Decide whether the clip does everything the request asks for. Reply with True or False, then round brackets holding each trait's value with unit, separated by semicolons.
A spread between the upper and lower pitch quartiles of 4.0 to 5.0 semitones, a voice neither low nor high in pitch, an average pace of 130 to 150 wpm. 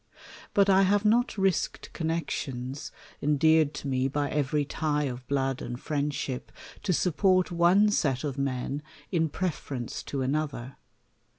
True (4.4 semitones; 150 Hz; 140 wpm)